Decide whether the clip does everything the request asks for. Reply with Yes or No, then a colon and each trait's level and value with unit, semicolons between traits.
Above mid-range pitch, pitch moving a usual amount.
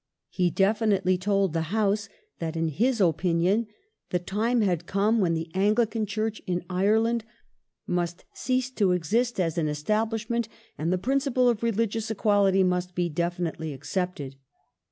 Yes: high, 195 Hz; average, 4.1 semitones